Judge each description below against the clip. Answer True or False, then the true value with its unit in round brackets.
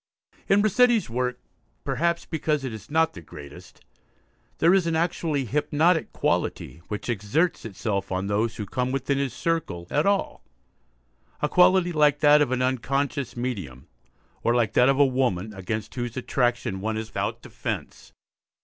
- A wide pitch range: True (6.3 semitones)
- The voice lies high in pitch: False (130 Hz)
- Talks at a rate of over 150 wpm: True (160 wpm)